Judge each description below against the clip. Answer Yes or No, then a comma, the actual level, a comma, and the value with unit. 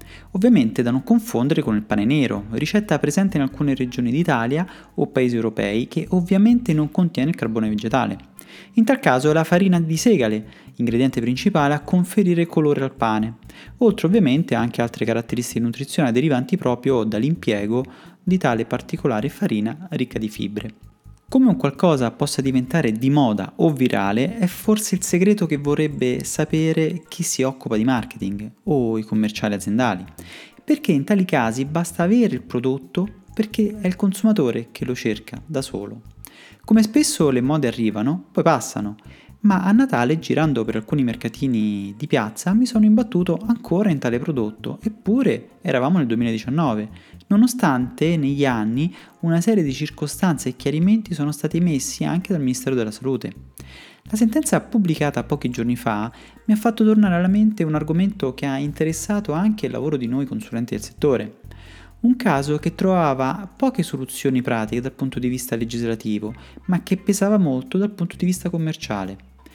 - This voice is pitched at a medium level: Yes, medium, 145 Hz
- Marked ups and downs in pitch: Yes, wide, 7.7 semitones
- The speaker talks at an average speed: Yes, average, 160 wpm